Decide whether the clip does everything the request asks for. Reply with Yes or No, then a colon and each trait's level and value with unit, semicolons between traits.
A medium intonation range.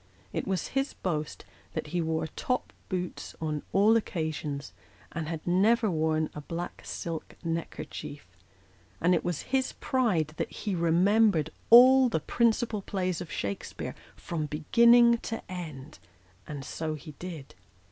No: wide, 5.8 semitones